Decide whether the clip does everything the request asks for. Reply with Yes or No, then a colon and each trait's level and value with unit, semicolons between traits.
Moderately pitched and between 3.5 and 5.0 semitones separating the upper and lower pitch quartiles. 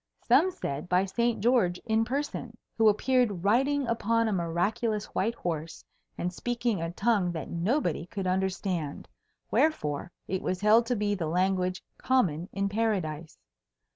No: high, 200 Hz; average, 4.7 semitones